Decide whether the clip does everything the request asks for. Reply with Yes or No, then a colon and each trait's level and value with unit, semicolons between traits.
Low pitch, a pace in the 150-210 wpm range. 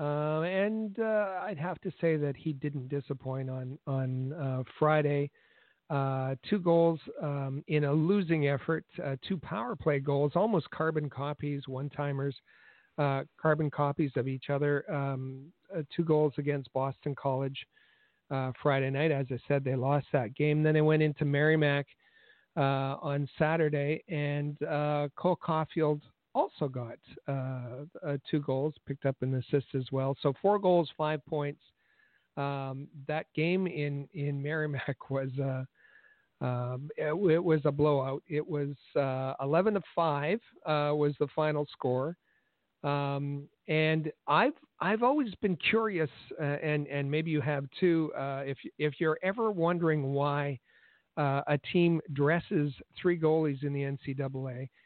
No: medium, 145 Hz; average, 155 wpm